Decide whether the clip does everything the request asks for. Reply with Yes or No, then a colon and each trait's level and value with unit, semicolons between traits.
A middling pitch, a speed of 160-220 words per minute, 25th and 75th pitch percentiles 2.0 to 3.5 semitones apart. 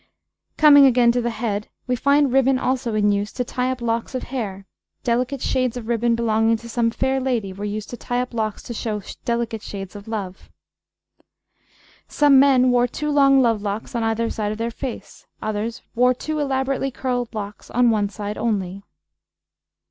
No: high, 235 Hz; average, 185 wpm; average, 3.0 semitones